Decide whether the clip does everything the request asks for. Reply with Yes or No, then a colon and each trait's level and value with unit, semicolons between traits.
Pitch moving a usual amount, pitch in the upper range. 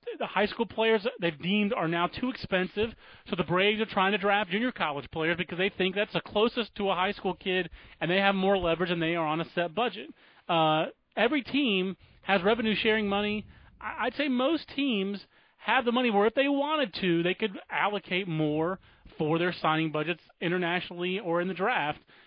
Yes: average, 4.1 semitones; high, 195 Hz